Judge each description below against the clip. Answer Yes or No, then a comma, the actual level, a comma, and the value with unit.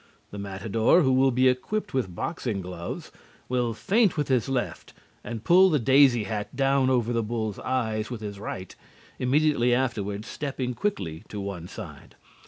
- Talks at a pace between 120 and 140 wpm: No, average, 165 wpm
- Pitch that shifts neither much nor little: Yes, average, 4.4 semitones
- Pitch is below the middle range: Yes, low, 120 Hz